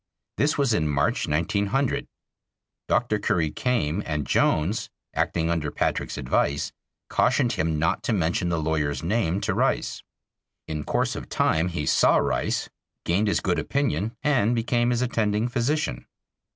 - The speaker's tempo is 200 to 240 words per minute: No, average, 145 wpm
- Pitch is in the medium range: No, very low, 95 Hz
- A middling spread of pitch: No, wide, 7.0 semitones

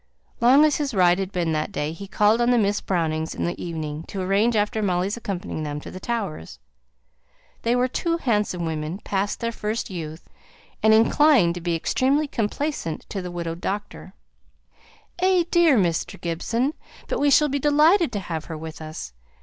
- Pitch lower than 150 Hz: No, high, 200 Hz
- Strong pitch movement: Yes, wide, 6.5 semitones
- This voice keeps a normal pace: Yes, average, 180 wpm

